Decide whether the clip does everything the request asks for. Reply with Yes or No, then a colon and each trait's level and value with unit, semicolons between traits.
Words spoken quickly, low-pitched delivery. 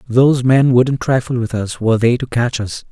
Yes: fast, 225 wpm; low, 120 Hz